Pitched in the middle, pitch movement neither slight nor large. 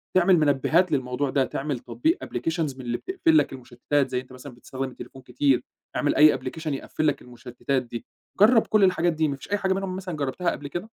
No: medium, 145 Hz; wide, 5.8 semitones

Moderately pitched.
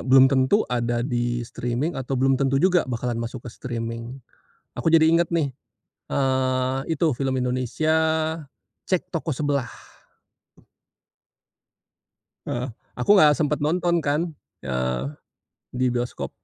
No: low, 130 Hz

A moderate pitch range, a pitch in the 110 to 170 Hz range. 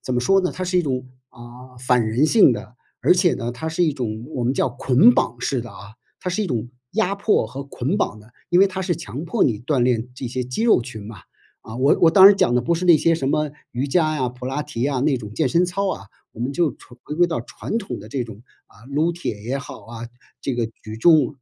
No: wide, 6.1 semitones; low, 135 Hz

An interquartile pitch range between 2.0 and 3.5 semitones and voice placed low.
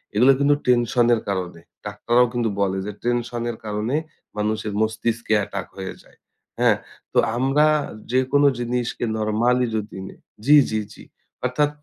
Yes: average, 2.8 semitones; low, 115 Hz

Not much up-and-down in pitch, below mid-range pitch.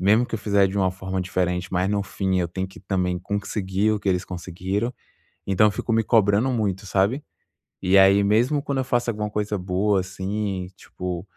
Yes: narrow, 2.2 semitones; low, 100 Hz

